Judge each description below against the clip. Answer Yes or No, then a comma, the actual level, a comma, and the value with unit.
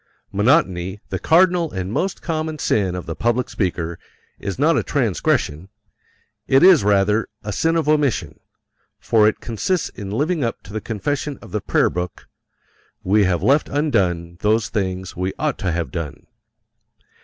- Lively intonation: Yes, wide, 7.7 semitones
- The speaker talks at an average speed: Yes, average, 160 wpm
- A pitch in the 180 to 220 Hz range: No, low, 105 Hz